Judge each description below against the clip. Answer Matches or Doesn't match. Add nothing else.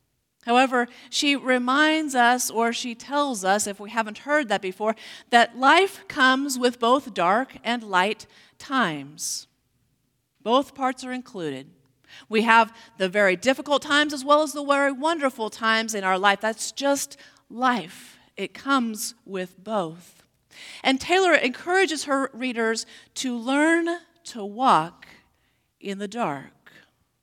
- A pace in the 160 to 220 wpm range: Doesn't match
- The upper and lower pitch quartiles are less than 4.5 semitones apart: Doesn't match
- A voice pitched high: Matches